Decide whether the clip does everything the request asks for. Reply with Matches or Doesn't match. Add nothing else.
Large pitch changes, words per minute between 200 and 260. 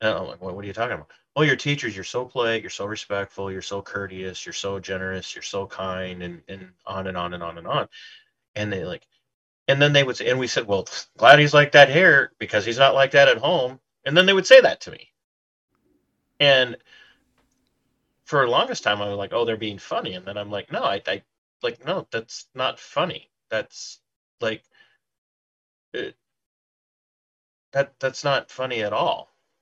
Matches